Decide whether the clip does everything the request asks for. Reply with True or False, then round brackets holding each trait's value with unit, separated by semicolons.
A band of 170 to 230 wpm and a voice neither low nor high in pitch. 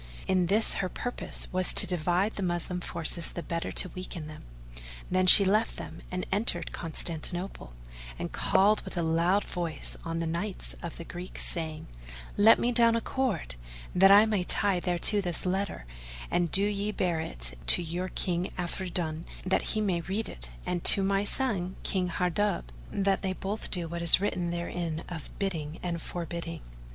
True (175 wpm; 180 Hz)